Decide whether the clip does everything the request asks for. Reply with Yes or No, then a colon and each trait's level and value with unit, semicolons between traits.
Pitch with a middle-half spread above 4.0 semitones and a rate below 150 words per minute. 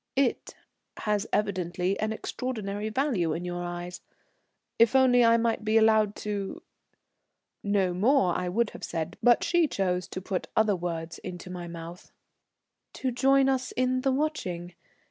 No: wide, 5.5 semitones; average, 155 wpm